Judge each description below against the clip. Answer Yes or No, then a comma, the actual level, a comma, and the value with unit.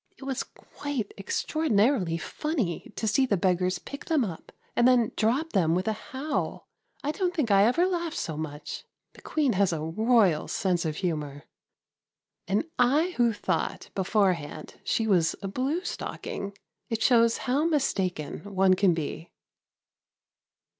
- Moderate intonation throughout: No, wide, 7.0 semitones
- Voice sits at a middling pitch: No, high, 210 Hz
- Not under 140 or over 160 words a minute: Yes, average, 150 wpm